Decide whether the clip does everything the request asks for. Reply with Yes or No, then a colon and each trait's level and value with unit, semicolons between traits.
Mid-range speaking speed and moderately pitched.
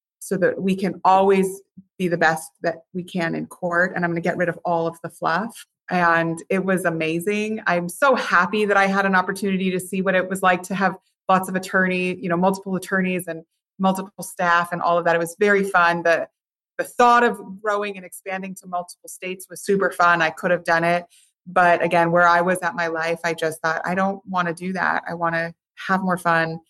No: fast, 230 wpm; medium, 180 Hz